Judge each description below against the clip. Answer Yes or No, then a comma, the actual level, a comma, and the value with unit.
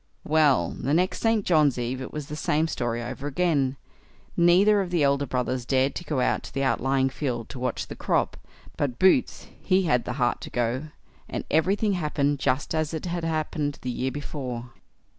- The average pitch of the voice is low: No, medium, 145 Hz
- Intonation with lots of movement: No, average, 4.1 semitones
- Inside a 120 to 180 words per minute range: No, average, 195 wpm